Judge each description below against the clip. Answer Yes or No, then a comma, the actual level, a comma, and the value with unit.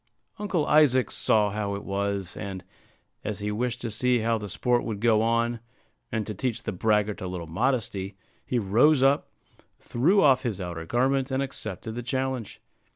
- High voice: No, low, 115 Hz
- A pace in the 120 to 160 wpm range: No, average, 175 wpm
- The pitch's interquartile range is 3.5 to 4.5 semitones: Yes, average, 4.2 semitones